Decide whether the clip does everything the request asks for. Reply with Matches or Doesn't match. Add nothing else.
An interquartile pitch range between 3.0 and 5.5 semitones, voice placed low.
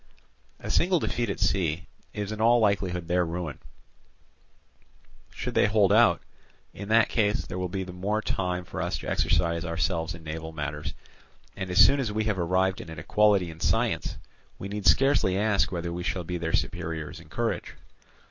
Matches